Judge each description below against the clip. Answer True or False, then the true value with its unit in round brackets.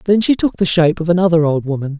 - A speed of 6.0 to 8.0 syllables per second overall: True (7.0 syllables/s)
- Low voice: False (170 Hz)